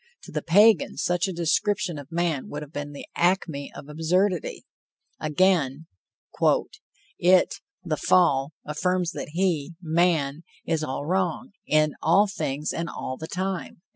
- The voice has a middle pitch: Yes, medium, 165 Hz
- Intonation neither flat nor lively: Yes, average, 3.4 semitones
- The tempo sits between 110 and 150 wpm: Yes, average, 140 wpm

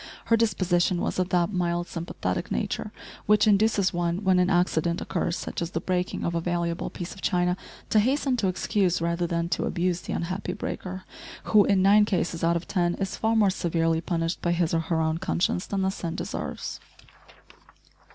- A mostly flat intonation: Yes, narrow, 2.3 semitones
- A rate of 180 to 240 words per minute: Yes, average, 190 wpm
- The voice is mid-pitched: Yes, medium, 180 Hz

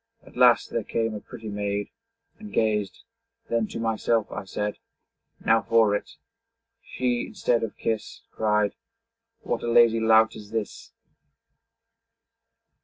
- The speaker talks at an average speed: No, slow, 130 wpm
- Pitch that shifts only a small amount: Yes, narrow, 1.6 semitones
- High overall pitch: No, low, 110 Hz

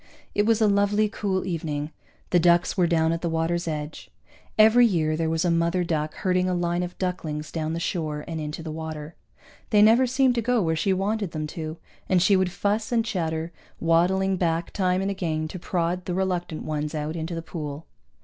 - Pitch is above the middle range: No, medium, 175 Hz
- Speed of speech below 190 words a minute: No, fast, 205 wpm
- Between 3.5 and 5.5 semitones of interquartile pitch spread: No, average, 3.1 semitones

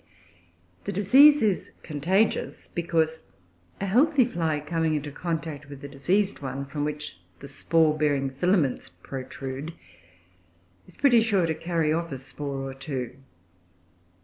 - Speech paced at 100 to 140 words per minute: Yes, slow, 135 wpm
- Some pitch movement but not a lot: Yes, average, 4.5 semitones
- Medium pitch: Yes, medium, 155 Hz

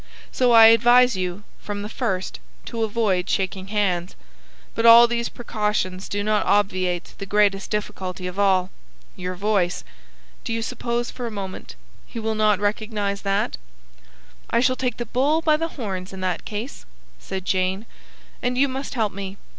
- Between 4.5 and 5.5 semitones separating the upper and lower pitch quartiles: No, average, 3.6 semitones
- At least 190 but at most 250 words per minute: No, average, 165 wpm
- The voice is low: No, high, 210 Hz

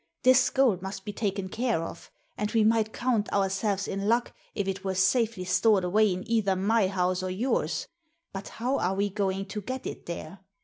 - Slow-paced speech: No, average, 195 wpm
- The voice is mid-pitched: No, high, 200 Hz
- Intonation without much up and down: No, average, 3.0 semitones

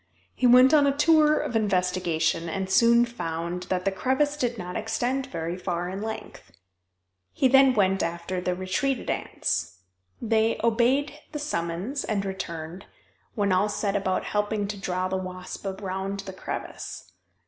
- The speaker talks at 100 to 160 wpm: Yes, average, 155 wpm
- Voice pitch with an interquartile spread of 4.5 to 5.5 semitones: Yes, average, 4.9 semitones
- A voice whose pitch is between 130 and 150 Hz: No, high, 200 Hz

